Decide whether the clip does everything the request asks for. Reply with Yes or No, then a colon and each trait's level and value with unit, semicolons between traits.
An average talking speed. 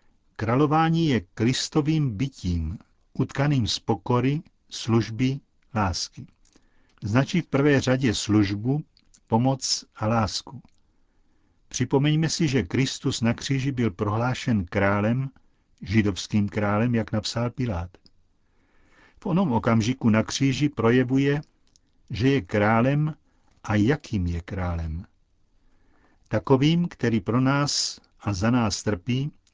No: slow, 105 wpm